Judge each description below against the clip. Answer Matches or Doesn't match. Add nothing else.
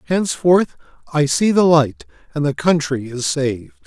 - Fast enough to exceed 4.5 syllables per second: Matches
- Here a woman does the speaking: Doesn't match